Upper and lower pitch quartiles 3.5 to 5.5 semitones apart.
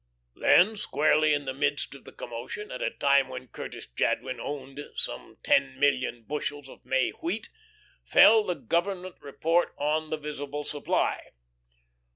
No: average, 2.9 semitones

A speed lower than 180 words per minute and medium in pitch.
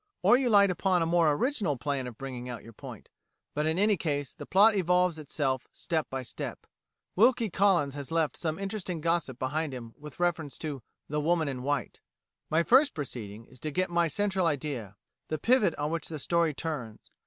No: average, 195 wpm; medium, 155 Hz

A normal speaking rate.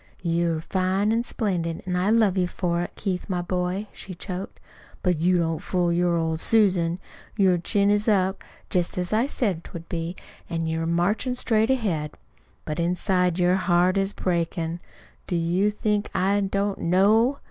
Yes: average, 170 wpm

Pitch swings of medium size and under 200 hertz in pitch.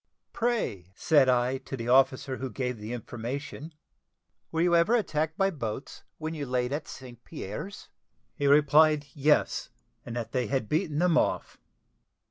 Yes: average, 4.2 semitones; medium, 140 Hz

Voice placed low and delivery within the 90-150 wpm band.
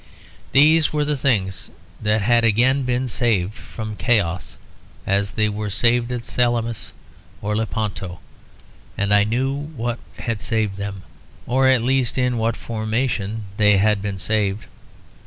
Yes: low, 110 Hz; average, 140 wpm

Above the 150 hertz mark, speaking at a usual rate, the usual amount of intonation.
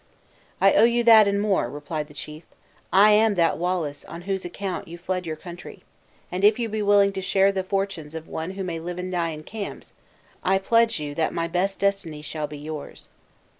No: medium, 185 Hz; fast, 210 wpm; average, 3.6 semitones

